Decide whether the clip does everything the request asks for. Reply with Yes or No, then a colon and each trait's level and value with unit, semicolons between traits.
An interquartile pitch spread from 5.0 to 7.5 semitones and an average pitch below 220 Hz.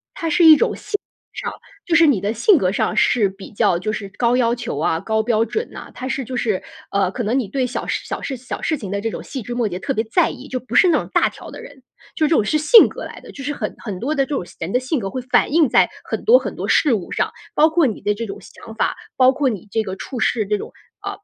No: wide, 5.5 semitones; high, 245 Hz